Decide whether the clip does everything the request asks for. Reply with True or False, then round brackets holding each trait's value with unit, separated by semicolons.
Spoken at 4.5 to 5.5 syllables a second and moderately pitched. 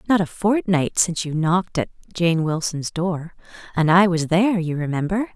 True (5.1 syllables/s; 175 Hz)